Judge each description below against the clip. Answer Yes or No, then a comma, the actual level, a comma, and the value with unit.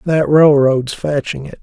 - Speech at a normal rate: Yes, average, 145 wpm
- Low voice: No, medium, 145 Hz